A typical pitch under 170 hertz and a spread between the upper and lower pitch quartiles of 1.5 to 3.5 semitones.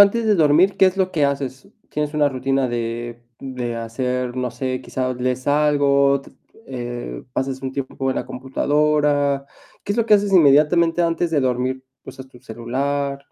Yes: medium, 140 Hz; average, 3.0 semitones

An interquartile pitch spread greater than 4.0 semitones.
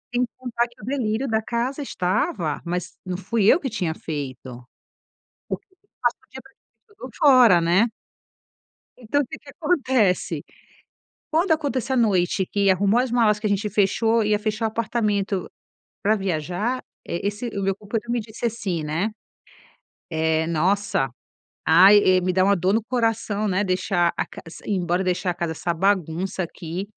Yes: average, 4.5 semitones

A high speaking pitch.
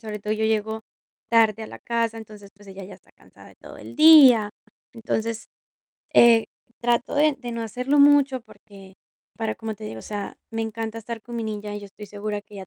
Yes: high, 220 Hz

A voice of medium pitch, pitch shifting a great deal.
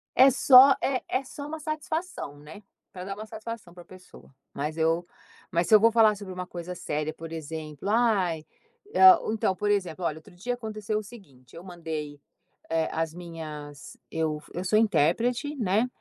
Yes: medium, 180 Hz; wide, 5.8 semitones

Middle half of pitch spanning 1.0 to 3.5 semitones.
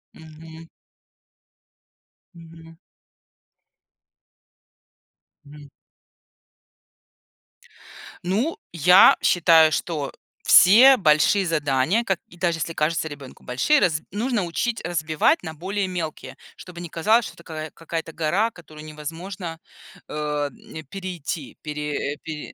Yes: average, 3.1 semitones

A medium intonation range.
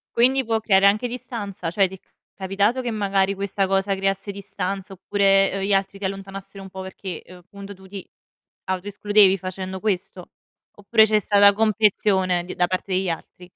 No: narrow, 1.3 semitones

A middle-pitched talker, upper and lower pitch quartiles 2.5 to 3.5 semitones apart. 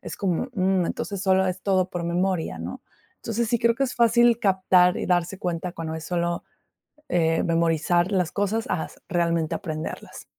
Yes: medium, 180 Hz; average, 2.8 semitones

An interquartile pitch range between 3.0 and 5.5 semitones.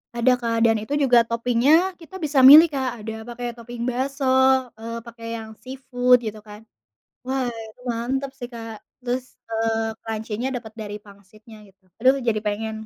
No: narrow, 2.6 semitones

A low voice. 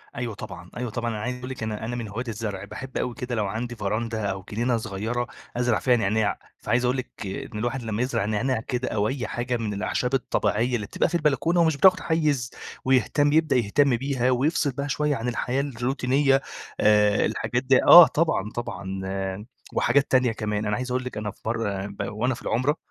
Yes: low, 120 Hz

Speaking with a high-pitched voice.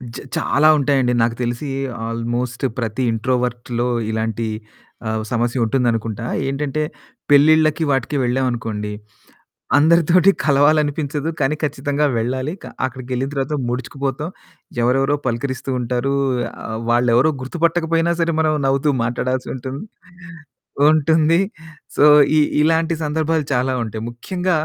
No: low, 135 Hz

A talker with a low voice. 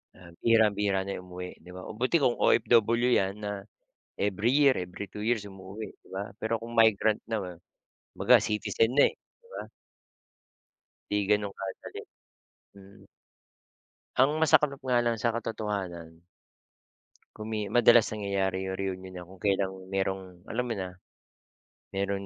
Yes: low, 105 Hz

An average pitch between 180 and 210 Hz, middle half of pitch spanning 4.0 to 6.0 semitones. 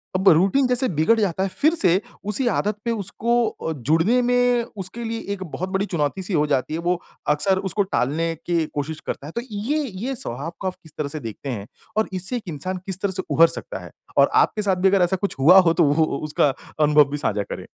Yes: medium, 185 Hz; average, 5.3 semitones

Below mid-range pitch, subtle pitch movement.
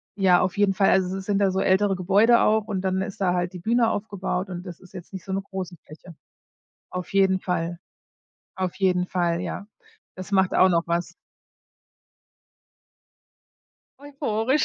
No: high, 190 Hz; narrow, 1.8 semitones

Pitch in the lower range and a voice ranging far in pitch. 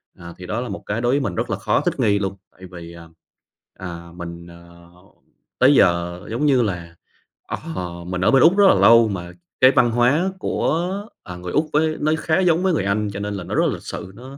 Yes: low, 100 Hz; wide, 8.0 semitones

